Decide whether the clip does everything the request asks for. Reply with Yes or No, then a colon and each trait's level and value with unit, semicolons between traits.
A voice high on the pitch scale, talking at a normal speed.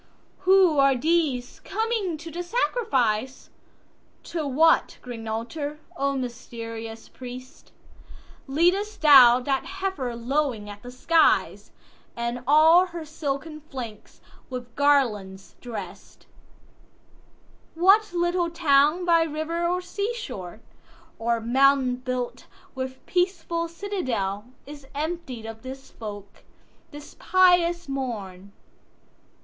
No: very high, 275 Hz; slow, 95 wpm